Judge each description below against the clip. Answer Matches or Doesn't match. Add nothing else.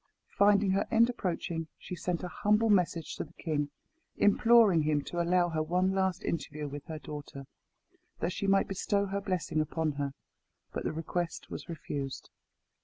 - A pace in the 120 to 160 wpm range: Doesn't match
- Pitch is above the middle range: Doesn't match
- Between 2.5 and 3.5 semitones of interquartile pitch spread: Doesn't match